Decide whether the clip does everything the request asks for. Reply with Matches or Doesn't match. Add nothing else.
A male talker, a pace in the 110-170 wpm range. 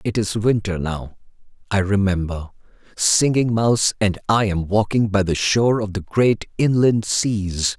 Matches